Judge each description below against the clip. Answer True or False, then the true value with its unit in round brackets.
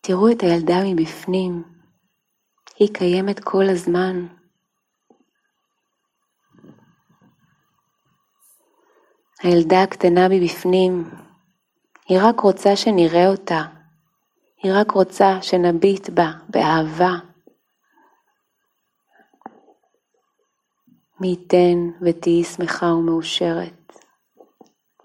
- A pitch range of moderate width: False (2.1 semitones)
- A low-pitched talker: False (185 Hz)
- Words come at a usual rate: False (65 wpm)